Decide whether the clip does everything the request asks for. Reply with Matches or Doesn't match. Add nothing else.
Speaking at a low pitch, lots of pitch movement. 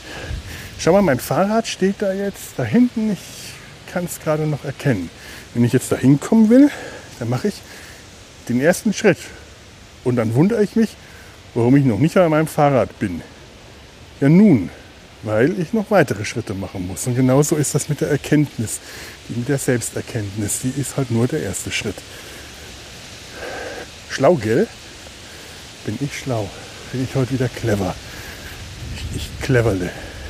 Matches